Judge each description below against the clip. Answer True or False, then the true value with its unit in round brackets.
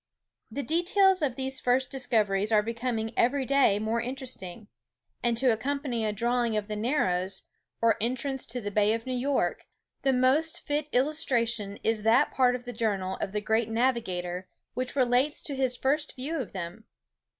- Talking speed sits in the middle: True (170 wpm)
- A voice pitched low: False (240 Hz)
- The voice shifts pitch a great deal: False (3.6 semitones)